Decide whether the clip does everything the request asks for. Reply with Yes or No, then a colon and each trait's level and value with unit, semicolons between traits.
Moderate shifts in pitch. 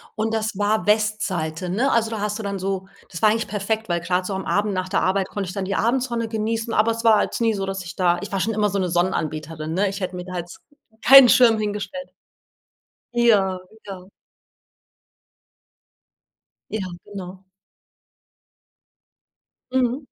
Yes: average, 3.1 semitones